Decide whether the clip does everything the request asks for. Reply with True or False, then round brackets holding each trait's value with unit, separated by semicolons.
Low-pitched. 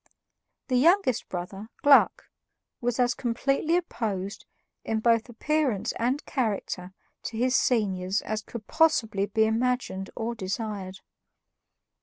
False (230 Hz)